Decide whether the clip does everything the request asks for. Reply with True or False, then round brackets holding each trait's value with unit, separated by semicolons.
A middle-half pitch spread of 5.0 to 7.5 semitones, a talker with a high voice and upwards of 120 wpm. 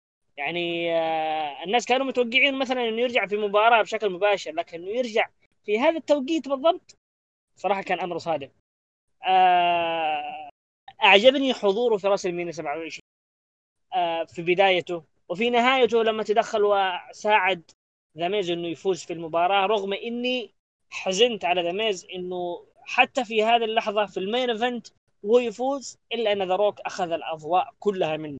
True (5.6 semitones; 205 Hz; 130 wpm)